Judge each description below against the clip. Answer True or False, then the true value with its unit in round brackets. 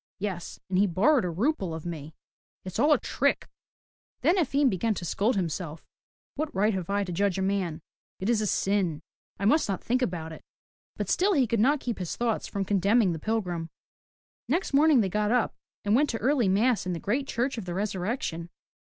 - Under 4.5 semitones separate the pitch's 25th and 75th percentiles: False (5.3 semitones)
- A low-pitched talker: False (205 Hz)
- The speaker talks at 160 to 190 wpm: False (205 wpm)